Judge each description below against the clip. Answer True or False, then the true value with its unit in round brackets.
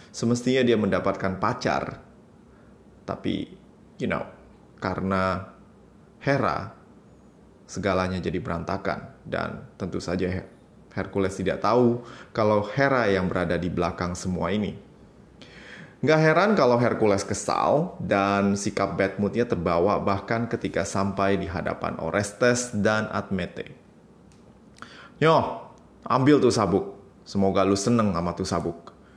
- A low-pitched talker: True (100 Hz)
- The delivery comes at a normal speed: True (110 wpm)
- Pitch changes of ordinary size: True (3.5 semitones)